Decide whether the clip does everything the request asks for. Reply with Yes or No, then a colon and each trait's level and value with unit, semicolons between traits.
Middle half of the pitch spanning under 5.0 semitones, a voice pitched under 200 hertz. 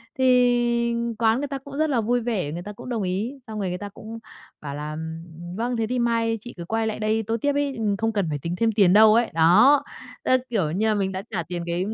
No: average, 4.6 semitones; high, 220 Hz